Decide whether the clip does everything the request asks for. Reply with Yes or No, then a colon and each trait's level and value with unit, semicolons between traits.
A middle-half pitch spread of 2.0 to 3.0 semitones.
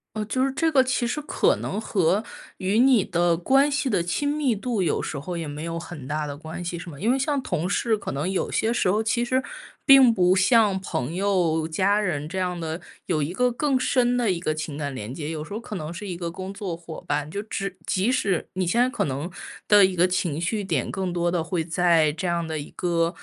No: average, 5.2 semitones